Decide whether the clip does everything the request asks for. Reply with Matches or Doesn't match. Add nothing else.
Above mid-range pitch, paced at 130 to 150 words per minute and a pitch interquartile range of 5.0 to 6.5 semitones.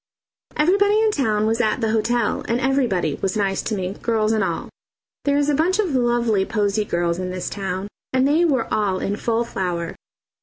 Doesn't match